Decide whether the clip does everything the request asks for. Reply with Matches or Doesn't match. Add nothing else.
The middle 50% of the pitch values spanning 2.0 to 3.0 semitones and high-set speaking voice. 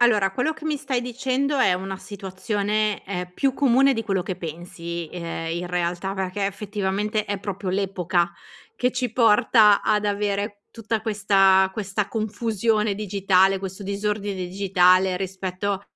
Matches